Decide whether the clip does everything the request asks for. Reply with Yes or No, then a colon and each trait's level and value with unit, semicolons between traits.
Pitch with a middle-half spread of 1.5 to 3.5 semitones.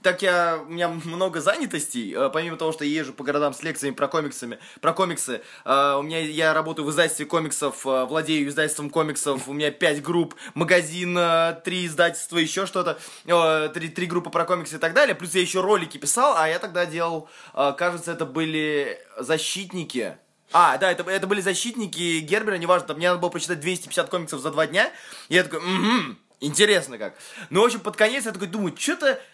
Yes: average, 2.7 semitones